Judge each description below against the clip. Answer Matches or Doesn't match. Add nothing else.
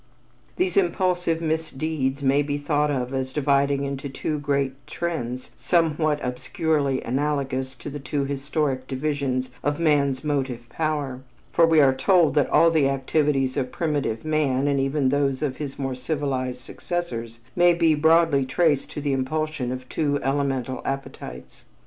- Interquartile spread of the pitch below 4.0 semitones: Matches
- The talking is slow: Doesn't match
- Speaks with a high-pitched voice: Doesn't match